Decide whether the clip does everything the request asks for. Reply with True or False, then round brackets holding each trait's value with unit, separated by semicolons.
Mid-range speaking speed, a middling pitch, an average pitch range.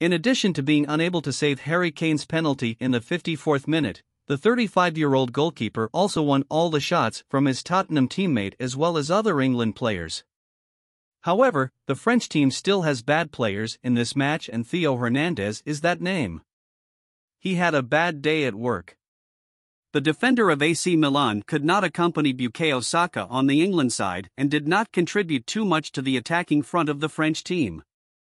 True (180 wpm; 150 Hz; 5.0 semitones)